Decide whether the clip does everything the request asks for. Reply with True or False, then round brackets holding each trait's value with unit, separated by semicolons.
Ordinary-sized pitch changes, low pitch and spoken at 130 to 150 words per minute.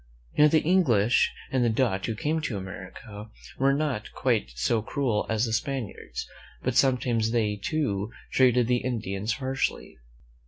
True (4.0 semitones; 120 Hz; 145 wpm)